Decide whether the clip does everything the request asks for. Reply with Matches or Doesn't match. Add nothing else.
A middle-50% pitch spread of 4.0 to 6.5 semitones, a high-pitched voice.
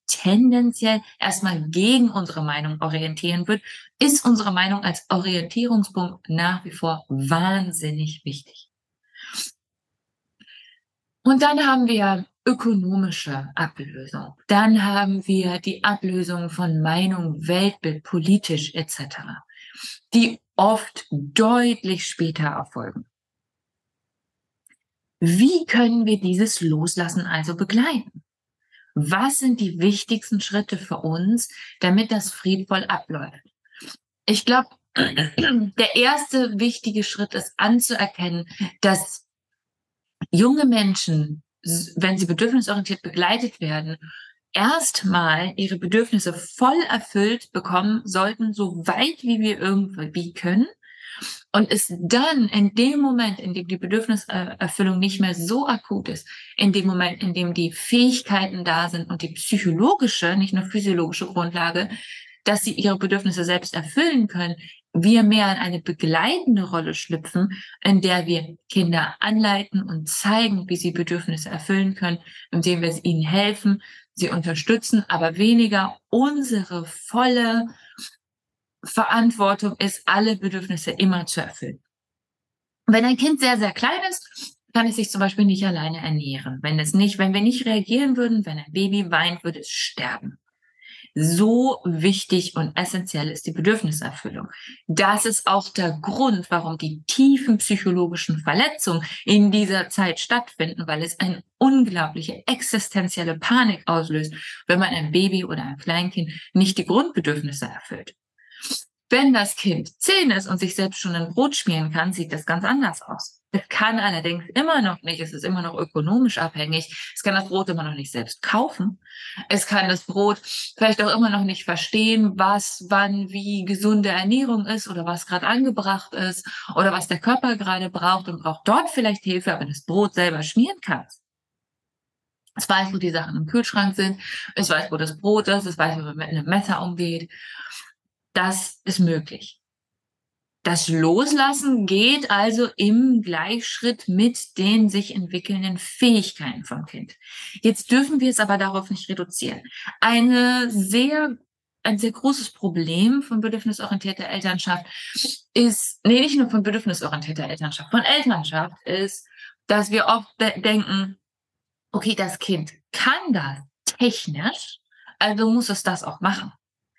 Matches